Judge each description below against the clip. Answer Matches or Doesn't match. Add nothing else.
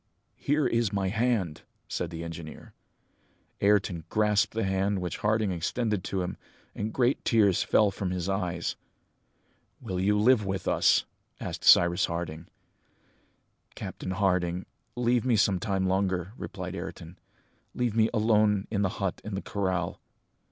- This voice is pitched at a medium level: Doesn't match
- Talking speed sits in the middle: Matches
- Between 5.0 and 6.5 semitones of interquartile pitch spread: Doesn't match